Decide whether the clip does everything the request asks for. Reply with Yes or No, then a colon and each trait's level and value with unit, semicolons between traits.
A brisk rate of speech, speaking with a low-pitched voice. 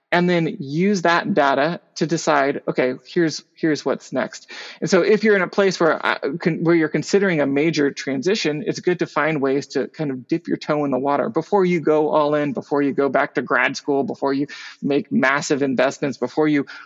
No: fast, 215 wpm; medium, 155 Hz